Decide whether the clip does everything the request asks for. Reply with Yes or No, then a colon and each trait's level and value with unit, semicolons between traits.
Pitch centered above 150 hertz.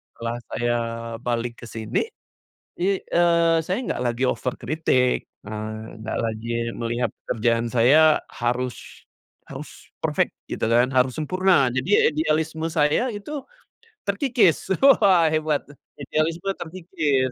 No: medium, 140 Hz